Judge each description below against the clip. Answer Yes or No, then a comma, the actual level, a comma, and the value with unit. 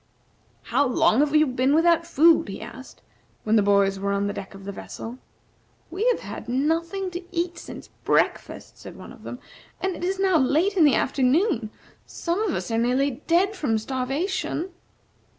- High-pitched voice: Yes, very high, 295 Hz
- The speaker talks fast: No, average, 185 wpm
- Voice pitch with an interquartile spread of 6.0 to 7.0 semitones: Yes, wide, 6.7 semitones